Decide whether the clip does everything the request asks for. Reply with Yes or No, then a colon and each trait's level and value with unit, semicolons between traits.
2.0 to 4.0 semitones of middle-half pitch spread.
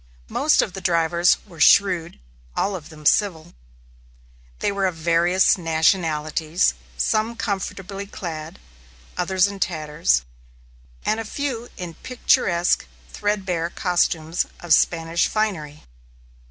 Yes: average, 3.5 semitones